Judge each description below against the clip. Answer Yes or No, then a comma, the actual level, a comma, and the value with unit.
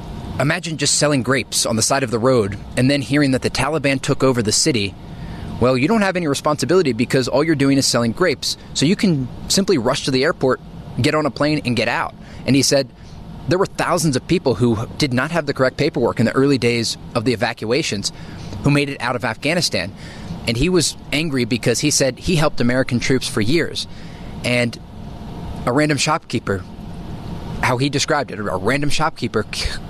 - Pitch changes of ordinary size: Yes, average, 3.7 semitones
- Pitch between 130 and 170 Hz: Yes, low, 135 Hz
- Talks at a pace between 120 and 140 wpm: No, average, 200 wpm